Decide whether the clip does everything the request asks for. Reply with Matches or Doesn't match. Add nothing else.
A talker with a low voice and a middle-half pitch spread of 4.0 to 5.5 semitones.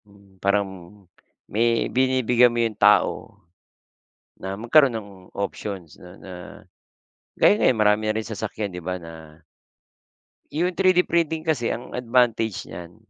Matches